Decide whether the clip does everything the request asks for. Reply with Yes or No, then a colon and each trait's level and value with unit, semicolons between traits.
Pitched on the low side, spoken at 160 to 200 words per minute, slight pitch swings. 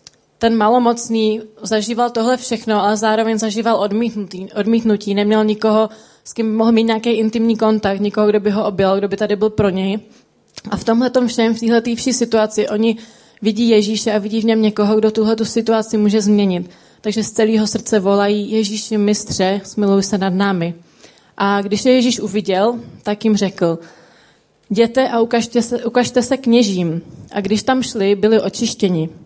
No: high, 215 Hz; fast, 170 wpm; narrow, 1.8 semitones